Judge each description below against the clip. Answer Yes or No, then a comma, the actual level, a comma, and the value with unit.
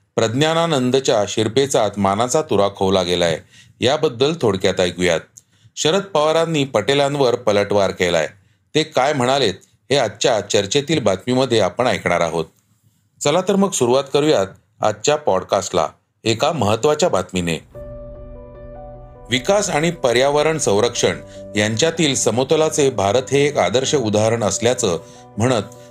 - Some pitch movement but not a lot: No, wide, 6.2 semitones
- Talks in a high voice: No, low, 120 Hz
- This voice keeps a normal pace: Yes, average, 110 wpm